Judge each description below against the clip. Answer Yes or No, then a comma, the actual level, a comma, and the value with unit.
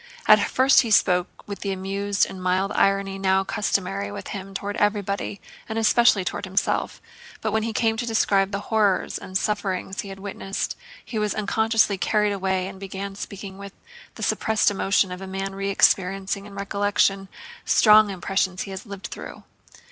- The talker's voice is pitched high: Yes, high, 195 Hz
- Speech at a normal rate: Yes, average, 175 wpm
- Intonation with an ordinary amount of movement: No, narrow, 1.4 semitones